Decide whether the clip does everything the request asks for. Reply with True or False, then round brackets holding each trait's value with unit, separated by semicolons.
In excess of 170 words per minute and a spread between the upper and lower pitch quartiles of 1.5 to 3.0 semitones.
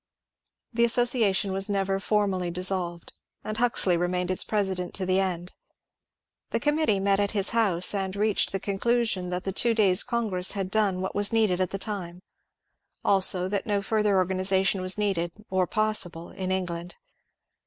False (165 wpm; 2.4 semitones)